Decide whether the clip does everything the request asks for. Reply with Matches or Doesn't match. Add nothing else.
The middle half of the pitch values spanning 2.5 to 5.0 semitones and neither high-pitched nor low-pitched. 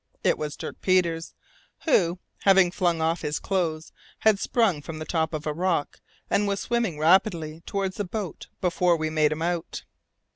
Matches